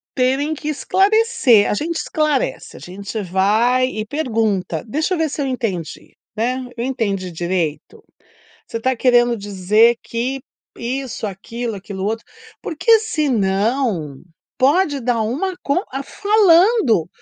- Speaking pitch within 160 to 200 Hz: No, high, 245 Hz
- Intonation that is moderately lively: No, wide, 6.0 semitones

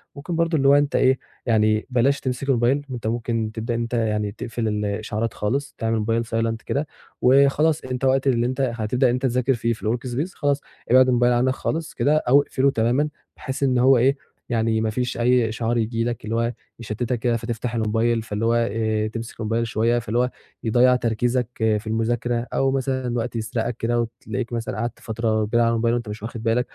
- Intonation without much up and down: Yes, narrow, 2.3 semitones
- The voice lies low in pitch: Yes, low, 120 Hz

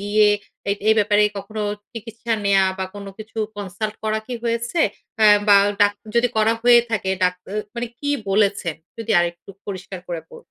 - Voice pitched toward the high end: Yes, high, 210 Hz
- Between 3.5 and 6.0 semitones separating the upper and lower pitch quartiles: No, narrow, 2.4 semitones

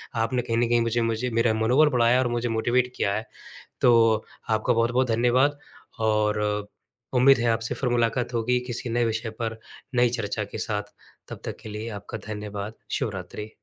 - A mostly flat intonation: Yes, narrow, 1.8 semitones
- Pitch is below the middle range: Yes, low, 115 Hz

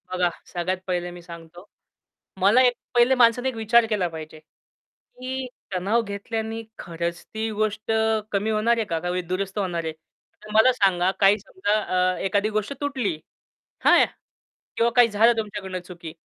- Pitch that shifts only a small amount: No, average, 4.1 semitones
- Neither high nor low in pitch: No, high, 200 Hz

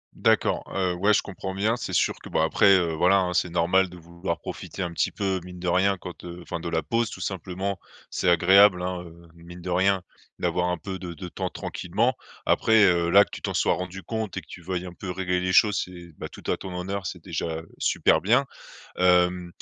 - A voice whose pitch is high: No, very low, 90 Hz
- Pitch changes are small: Yes, narrow, 1.7 semitones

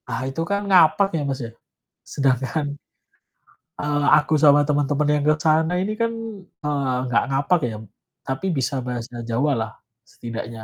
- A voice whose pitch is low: No, medium, 145 Hz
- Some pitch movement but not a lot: Yes, average, 3.3 semitones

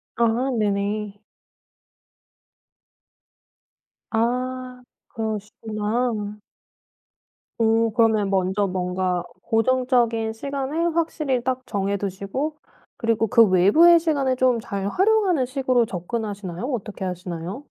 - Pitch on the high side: Yes, high, 225 Hz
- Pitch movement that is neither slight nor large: Yes, average, 4.3 semitones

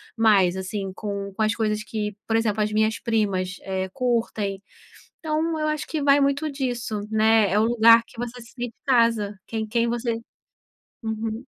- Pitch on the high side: Yes, high, 225 Hz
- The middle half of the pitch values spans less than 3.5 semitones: Yes, narrow, 2.4 semitones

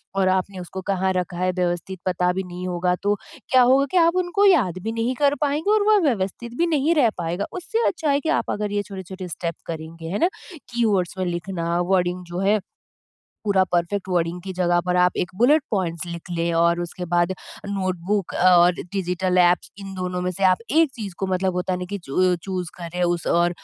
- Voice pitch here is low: No, medium, 185 Hz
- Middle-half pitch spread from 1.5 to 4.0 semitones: Yes, average, 2.8 semitones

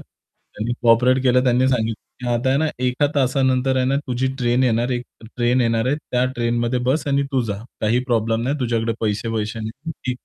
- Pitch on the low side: Yes, low, 125 Hz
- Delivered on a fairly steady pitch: Yes, narrow, 2.2 semitones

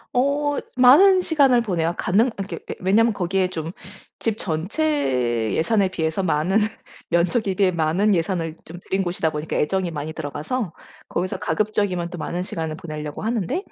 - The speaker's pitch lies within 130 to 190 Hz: Yes, medium, 185 Hz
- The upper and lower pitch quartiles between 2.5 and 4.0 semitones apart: No, average, 5.3 semitones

